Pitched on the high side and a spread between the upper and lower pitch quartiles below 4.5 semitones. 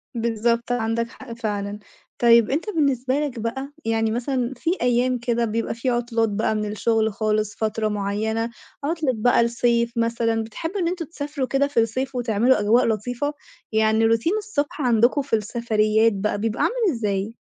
Yes: high, 235 Hz; average, 2.9 semitones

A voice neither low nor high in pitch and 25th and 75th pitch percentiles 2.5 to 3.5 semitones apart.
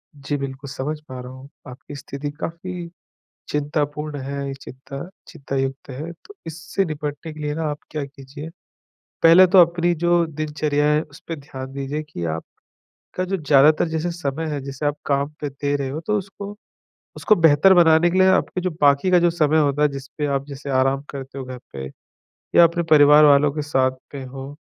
Yes: medium, 150 Hz; average, 3.1 semitones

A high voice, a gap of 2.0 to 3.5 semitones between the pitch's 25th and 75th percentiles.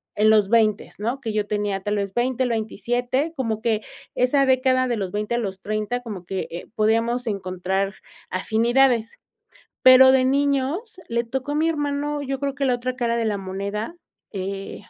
No: high, 235 Hz; average, 3.9 semitones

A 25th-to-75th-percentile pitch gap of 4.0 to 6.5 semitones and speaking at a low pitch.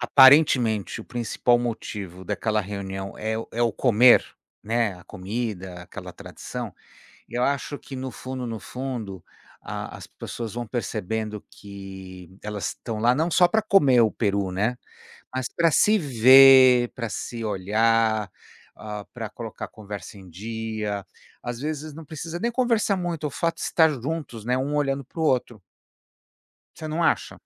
Yes: average, 4.6 semitones; low, 115 Hz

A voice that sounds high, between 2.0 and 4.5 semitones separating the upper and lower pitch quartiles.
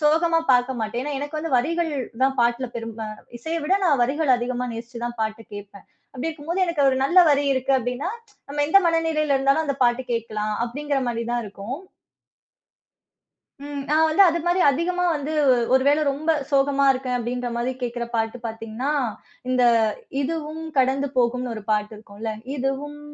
Yes: very high, 265 Hz; average, 4.1 semitones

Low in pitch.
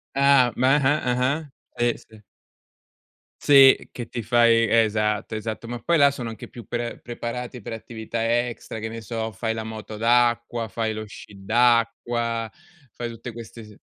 Yes: low, 115 Hz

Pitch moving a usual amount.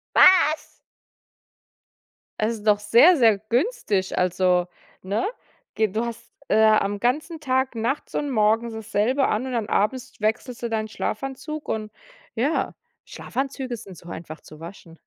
Yes: average, 4.0 semitones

